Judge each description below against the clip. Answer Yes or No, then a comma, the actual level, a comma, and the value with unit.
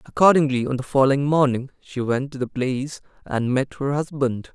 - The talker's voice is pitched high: No, low, 135 Hz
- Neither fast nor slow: Yes, average, 185 wpm